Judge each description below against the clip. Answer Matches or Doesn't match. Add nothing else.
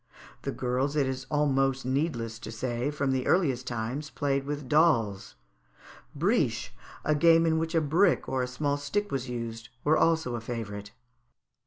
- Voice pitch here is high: Doesn't match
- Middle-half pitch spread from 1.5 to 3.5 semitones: Doesn't match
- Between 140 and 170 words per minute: Matches